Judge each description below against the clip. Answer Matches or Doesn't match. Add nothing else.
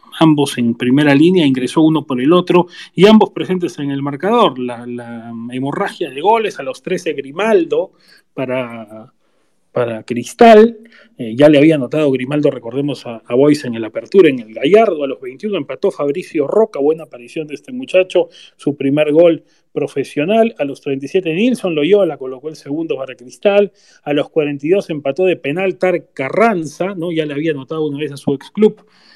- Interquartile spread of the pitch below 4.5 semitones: Doesn't match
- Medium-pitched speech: Matches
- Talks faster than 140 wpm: Matches